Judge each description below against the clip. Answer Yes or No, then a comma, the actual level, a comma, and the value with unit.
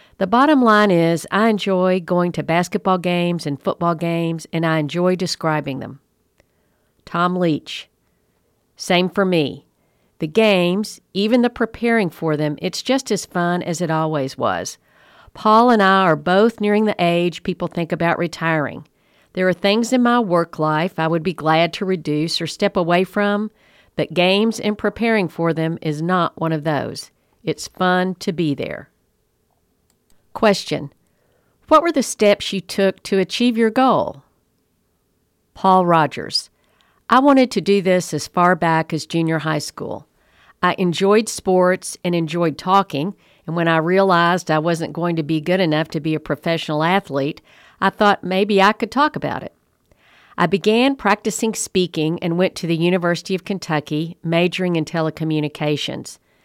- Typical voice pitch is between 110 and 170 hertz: No, medium, 180 Hz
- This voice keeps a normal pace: Yes, average, 160 wpm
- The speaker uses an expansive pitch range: No, average, 3.7 semitones